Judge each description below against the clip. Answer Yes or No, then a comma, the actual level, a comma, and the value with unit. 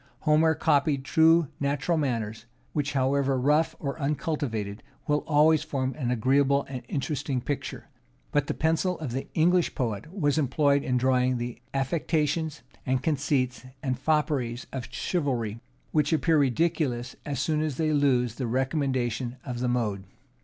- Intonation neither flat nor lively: Yes, average, 3.3 semitones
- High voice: No, medium, 140 Hz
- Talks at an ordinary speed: Yes, average, 145 wpm